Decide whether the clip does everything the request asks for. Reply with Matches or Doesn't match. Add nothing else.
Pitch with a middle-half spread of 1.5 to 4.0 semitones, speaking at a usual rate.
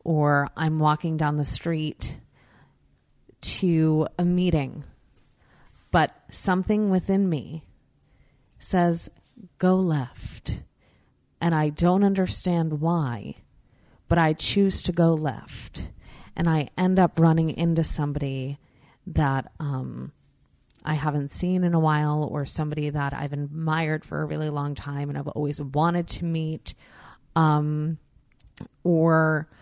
Doesn't match